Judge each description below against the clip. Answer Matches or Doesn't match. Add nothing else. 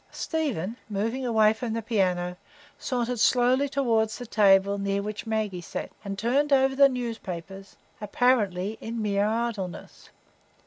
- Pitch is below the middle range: Doesn't match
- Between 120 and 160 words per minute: Matches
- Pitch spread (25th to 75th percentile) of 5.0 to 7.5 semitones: Doesn't match